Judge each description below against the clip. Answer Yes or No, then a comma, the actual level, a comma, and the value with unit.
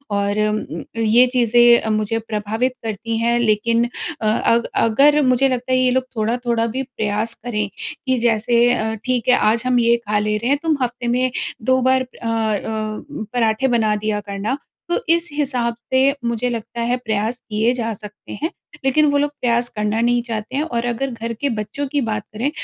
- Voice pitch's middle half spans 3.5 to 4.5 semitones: No, average, 2.7 semitones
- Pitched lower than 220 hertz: No, high, 235 Hz